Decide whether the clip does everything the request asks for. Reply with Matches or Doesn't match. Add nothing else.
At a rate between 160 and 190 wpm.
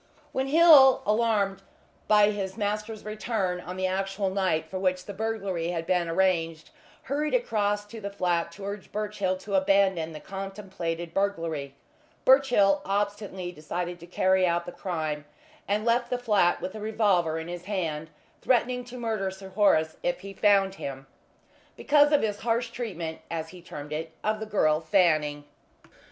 Matches